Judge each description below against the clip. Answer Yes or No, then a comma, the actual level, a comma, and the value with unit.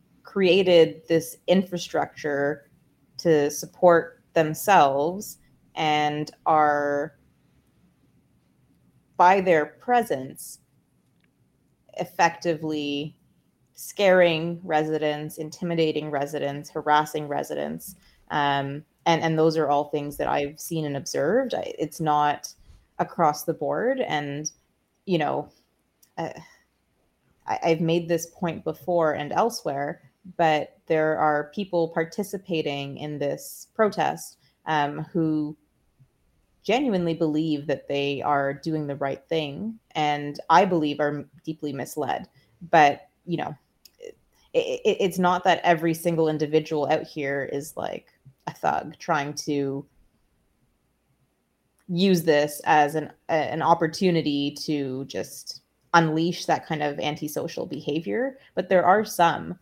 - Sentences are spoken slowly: Yes, slow, 110 wpm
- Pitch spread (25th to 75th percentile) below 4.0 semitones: Yes, average, 2.7 semitones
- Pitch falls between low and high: Yes, medium, 155 Hz